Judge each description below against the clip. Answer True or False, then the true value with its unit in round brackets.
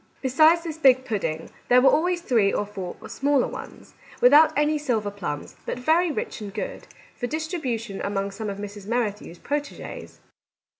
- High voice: True (245 Hz)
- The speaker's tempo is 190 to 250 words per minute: False (160 wpm)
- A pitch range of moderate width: False (6.7 semitones)